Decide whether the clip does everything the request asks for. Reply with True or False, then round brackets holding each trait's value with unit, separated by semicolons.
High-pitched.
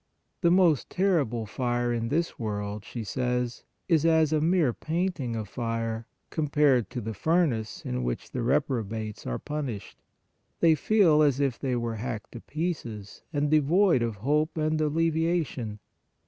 False (135 Hz)